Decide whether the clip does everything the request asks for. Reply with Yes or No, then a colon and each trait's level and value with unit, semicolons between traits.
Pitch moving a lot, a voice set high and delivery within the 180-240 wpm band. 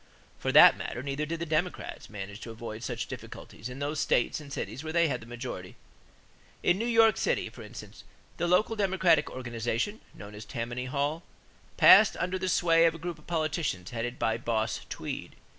No: wide, 6.5 semitones; medium, 145 Hz; average, 190 wpm